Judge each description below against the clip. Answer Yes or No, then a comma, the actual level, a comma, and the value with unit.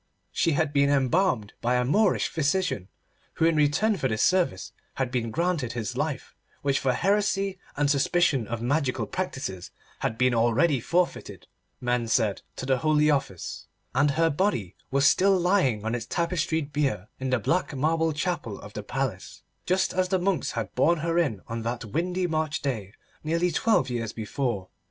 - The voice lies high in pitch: No, medium, 145 Hz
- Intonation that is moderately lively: No, wide, 6.2 semitones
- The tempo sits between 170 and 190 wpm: Yes, average, 175 wpm